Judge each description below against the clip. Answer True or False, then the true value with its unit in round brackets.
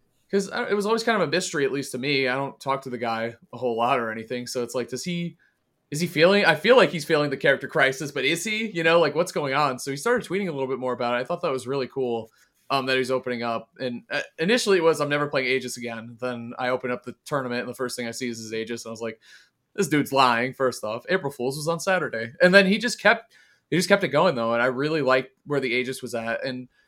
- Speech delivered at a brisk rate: True (290 wpm)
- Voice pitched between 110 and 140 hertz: True (135 Hz)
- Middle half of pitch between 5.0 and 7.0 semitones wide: True (5.4 semitones)